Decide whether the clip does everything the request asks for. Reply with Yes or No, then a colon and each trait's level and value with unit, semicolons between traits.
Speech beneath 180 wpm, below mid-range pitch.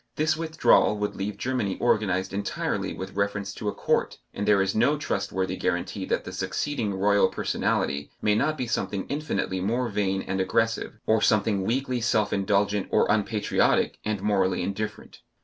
Yes: average, 165 wpm; low, 105 Hz